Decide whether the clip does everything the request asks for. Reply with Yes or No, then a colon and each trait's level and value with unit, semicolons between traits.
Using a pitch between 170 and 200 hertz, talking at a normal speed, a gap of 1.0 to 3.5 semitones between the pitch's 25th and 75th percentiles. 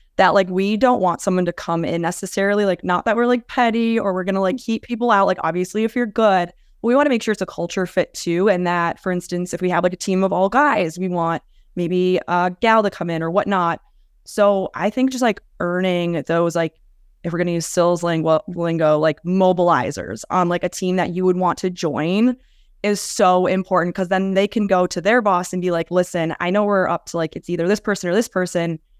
No: medium, 185 Hz; fast, 245 wpm; average, 2.8 semitones